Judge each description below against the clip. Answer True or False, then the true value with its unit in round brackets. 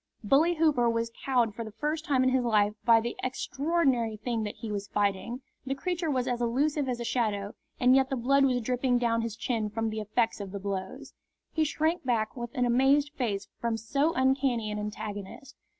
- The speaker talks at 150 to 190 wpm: False (205 wpm)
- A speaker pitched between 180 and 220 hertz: False (240 Hz)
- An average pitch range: True (3.7 semitones)